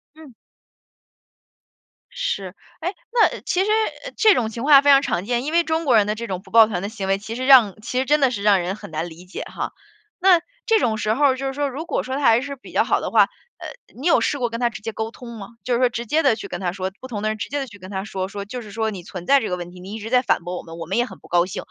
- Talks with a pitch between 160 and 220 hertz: No, high, 230 Hz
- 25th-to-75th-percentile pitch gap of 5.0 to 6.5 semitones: Yes, wide, 5.6 semitones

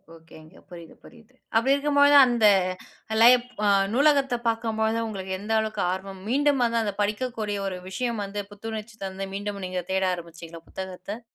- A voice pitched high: Yes, high, 215 Hz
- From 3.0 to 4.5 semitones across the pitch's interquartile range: Yes, average, 4.2 semitones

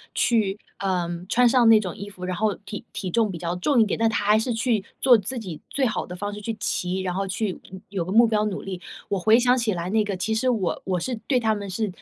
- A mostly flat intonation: No, average, 3.3 semitones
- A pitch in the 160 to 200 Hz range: No, high, 210 Hz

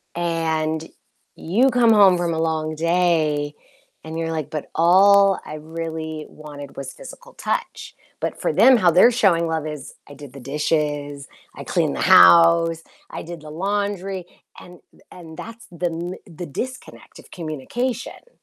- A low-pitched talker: No, medium, 165 Hz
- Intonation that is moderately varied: Yes, average, 3.5 semitones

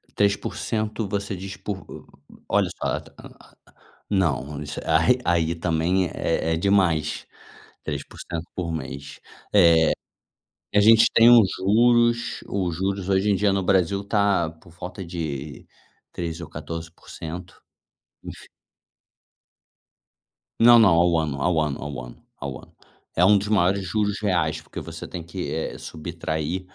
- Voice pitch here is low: Yes, very low, 90 Hz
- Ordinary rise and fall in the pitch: Yes, average, 3.7 semitones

